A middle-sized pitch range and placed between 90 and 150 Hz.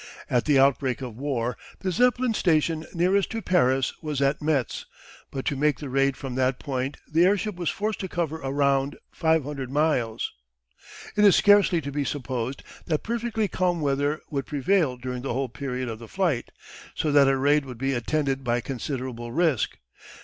Yes: average, 4.2 semitones; medium, 140 Hz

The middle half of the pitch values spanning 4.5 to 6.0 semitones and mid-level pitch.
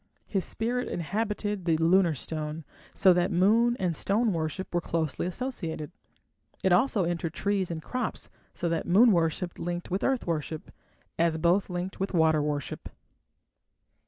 No: average, 3.6 semitones; medium, 175 Hz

